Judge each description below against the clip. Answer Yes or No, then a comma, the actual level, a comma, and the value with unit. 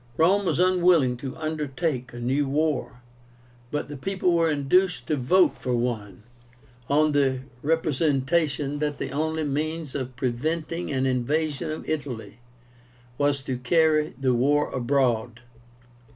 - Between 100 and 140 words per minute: Yes, slow, 135 wpm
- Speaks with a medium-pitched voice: Yes, medium, 145 Hz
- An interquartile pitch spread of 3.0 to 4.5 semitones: Yes, average, 3.7 semitones